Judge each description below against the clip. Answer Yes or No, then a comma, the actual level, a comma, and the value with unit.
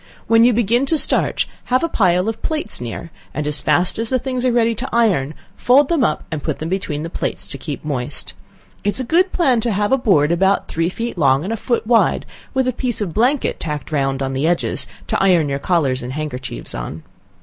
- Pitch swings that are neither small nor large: No, wide, 8.2 semitones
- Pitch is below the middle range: No, high, 190 Hz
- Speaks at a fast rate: Yes, fast, 230 wpm